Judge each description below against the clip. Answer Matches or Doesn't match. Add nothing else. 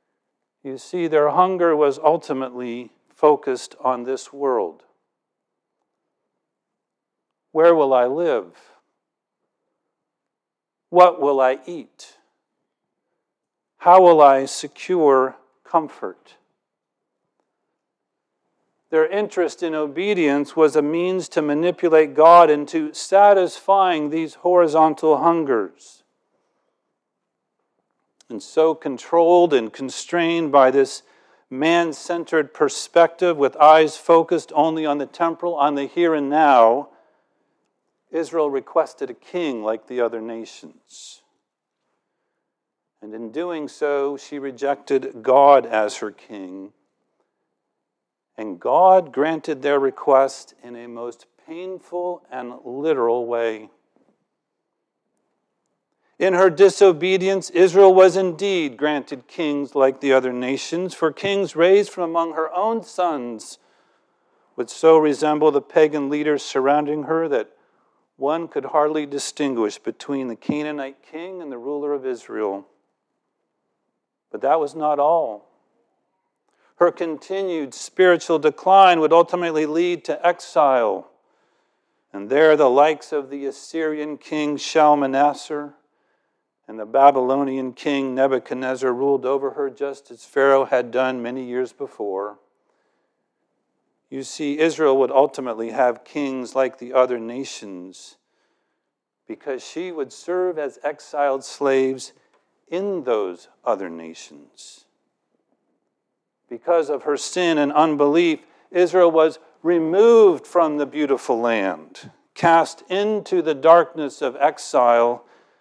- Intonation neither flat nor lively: Matches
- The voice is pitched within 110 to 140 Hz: Doesn't match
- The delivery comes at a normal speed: Doesn't match